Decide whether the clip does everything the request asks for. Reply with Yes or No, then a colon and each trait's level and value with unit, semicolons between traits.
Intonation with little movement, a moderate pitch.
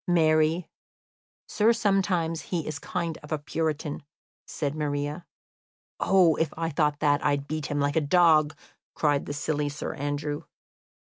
Yes: narrow, 2.1 semitones; medium, 155 Hz